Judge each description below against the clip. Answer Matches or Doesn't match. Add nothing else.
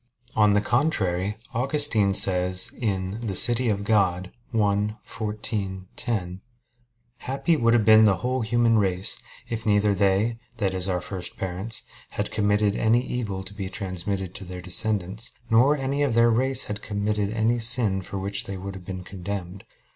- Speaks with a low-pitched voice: Matches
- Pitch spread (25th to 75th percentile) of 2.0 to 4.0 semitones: Matches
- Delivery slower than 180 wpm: Matches